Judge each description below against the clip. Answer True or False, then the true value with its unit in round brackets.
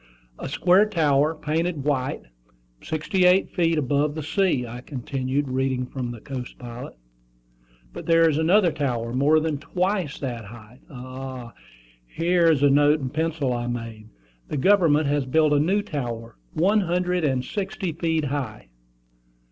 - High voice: False (145 Hz)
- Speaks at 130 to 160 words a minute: True (155 wpm)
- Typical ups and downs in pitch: True (4.5 semitones)